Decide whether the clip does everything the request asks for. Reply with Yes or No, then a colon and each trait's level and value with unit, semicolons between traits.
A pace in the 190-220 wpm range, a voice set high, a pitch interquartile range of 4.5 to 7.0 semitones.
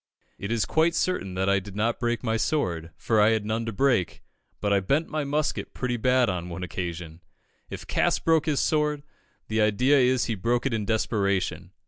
No: average, 200 wpm; low, 115 Hz; average, 5.3 semitones